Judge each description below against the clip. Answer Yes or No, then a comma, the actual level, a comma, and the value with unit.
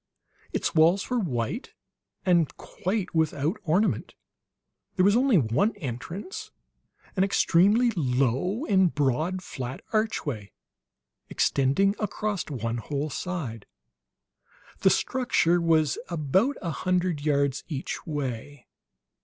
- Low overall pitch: No, medium, 165 Hz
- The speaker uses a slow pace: Yes, slow, 105 wpm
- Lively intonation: Yes, wide, 6.0 semitones